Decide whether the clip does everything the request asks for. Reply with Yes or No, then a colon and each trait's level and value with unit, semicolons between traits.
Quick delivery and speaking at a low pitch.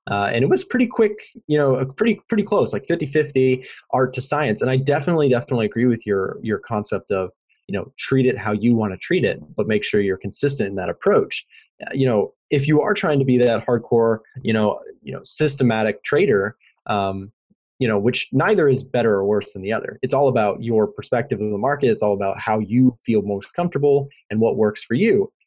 Yes: fast, 220 wpm; low, 125 Hz